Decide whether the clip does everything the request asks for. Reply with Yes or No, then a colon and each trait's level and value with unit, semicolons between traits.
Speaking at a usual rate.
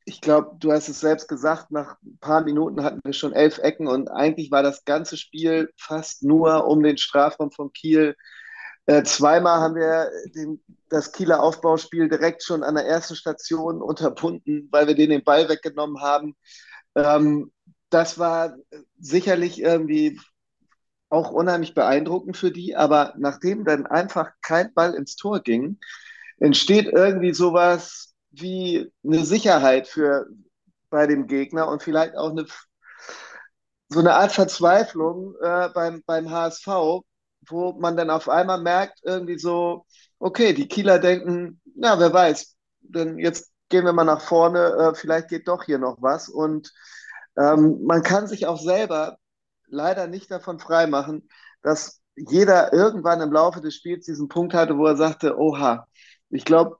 Yes: average, 155 wpm